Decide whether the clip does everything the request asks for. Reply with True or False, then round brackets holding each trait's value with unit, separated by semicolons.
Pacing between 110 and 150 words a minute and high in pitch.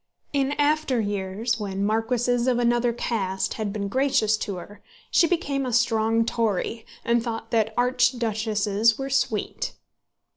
True (140 wpm; 230 Hz)